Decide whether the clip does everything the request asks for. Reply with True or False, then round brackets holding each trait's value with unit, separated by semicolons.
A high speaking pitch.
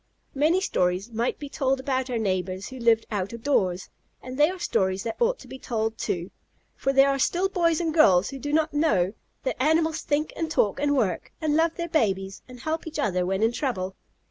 True (260 Hz)